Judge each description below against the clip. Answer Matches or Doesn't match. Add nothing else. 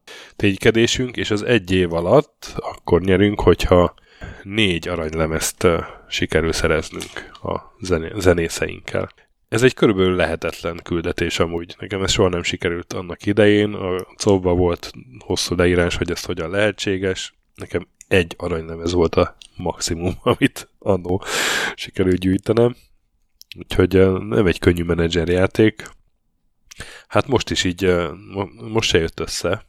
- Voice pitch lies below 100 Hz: Matches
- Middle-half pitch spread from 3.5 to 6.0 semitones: Doesn't match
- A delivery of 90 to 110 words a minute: Doesn't match